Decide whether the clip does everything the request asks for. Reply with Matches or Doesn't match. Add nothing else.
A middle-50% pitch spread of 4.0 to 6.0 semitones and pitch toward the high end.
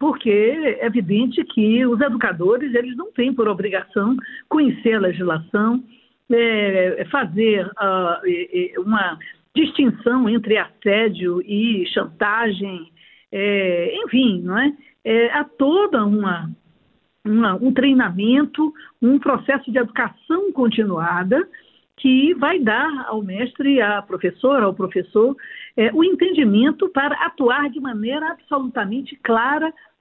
Matches